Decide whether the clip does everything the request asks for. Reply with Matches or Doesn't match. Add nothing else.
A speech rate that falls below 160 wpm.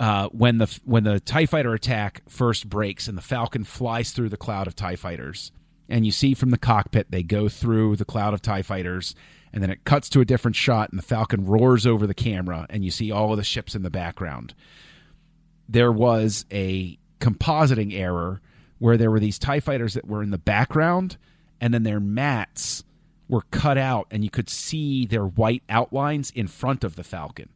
Doesn't match